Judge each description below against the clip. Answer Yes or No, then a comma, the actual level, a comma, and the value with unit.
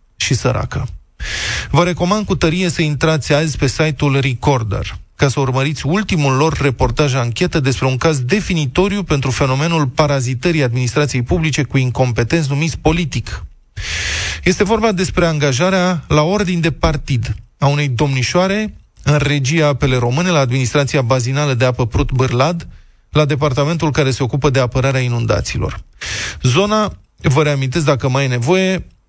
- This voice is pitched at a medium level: Yes, medium, 145 Hz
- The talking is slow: No, average, 140 wpm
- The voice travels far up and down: No, average, 4.0 semitones